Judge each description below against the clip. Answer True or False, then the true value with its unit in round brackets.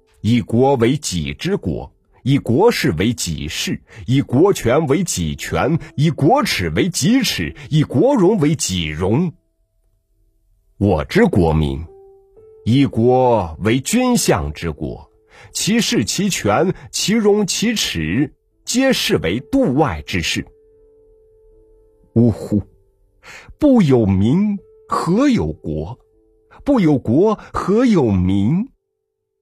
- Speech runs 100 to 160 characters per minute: True (145 characters per minute)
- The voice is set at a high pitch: False (140 Hz)